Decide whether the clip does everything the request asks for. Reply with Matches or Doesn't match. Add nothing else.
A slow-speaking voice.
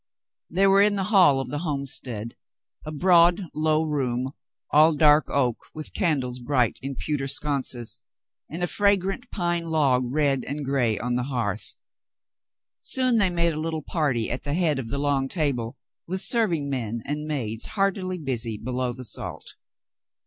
Doesn't match